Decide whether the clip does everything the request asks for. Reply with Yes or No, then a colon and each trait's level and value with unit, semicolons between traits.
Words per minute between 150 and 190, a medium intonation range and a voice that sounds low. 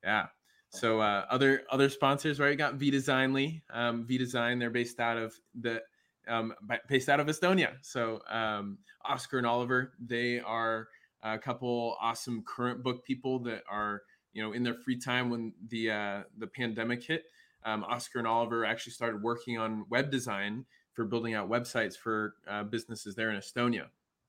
No: average, 175 wpm; narrow, 2.2 semitones; low, 120 Hz